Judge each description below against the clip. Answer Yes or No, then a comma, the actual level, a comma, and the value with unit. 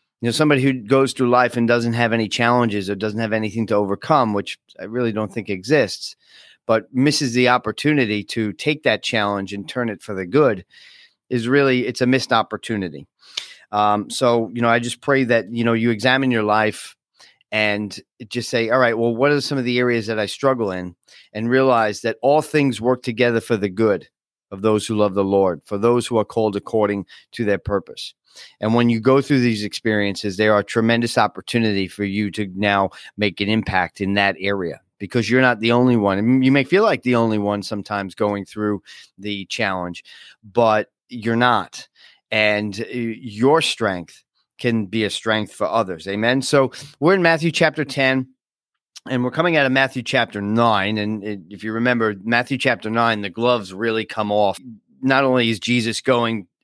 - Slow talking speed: No, average, 195 wpm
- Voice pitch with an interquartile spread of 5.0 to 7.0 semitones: No, average, 3.2 semitones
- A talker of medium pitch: No, low, 115 Hz